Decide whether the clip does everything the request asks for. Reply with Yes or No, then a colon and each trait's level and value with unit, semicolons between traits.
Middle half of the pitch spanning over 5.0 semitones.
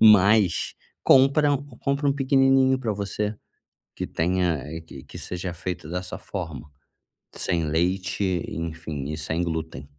Yes: wide, 5.4 semitones